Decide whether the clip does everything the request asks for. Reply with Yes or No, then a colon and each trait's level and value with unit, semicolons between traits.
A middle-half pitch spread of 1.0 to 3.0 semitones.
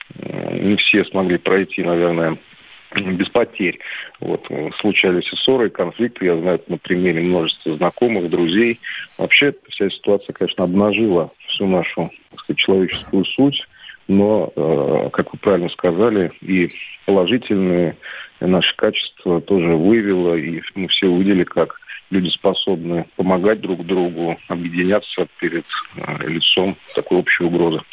Yes: average, 2.7 semitones